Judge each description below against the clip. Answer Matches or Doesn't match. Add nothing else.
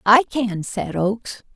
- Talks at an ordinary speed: Matches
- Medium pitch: Doesn't match